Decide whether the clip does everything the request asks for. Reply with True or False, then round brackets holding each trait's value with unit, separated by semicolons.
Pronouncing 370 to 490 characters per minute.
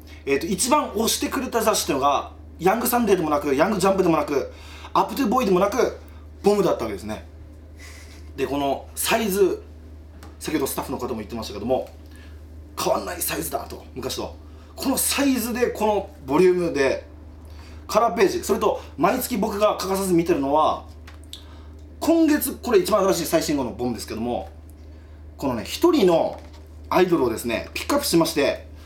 True (375 characters per minute)